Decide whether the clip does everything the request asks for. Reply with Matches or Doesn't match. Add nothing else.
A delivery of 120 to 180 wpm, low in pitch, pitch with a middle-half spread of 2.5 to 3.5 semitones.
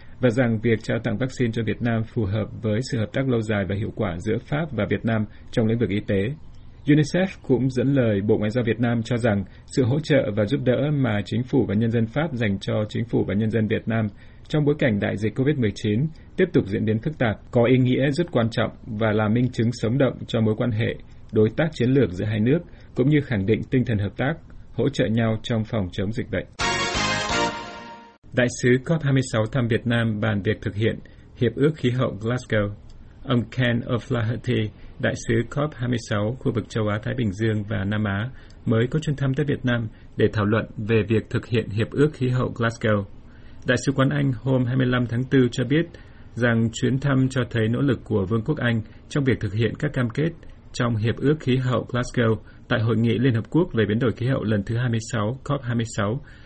Doesn't match